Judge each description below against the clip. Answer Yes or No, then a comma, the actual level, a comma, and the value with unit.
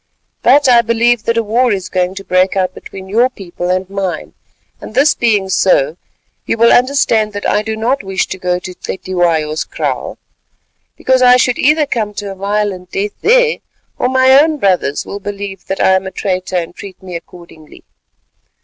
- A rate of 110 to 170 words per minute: No, average, 185 wpm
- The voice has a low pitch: No, high, 200 Hz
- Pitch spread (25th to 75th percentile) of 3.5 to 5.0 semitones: Yes, average, 4.3 semitones